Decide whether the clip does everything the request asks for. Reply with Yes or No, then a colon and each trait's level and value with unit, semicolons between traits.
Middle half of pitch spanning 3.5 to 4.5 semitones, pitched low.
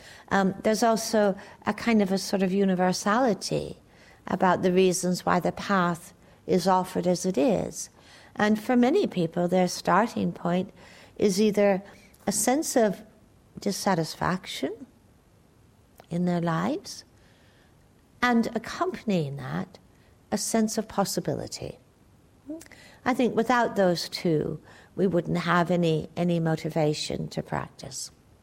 No: average, 3.9 semitones; medium, 185 Hz